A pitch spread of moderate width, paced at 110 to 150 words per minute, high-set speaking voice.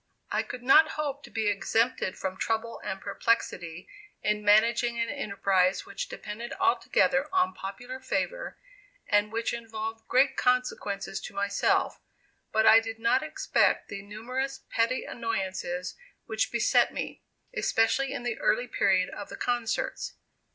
Yes: average, 3.7 semitones; average, 140 wpm; high, 225 Hz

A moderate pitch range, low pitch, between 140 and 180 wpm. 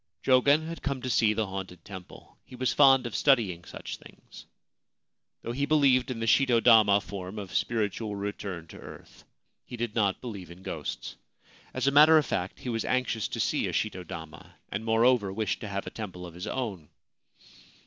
No: average, 4.8 semitones; low, 110 Hz; average, 190 wpm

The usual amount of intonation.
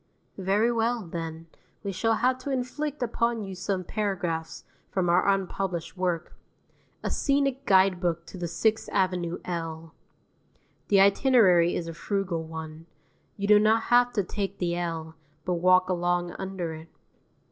Yes: average, 3.9 semitones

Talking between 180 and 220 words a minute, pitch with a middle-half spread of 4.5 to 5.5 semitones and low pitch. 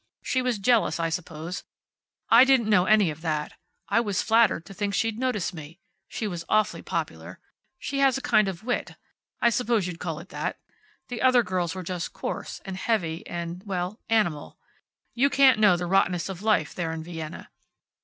No: average, 185 wpm; average, 5.1 semitones; high, 190 Hz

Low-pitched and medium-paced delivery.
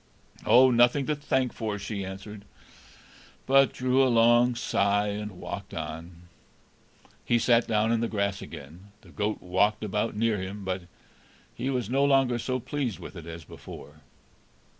Yes: low, 105 Hz; average, 160 wpm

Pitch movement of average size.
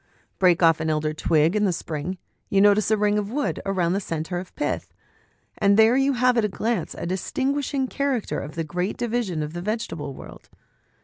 No: wide, 5.7 semitones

